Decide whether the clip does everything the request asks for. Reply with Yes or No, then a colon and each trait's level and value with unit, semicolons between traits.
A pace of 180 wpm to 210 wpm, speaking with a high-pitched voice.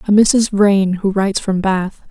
Yes: average, 200 wpm; high, 200 Hz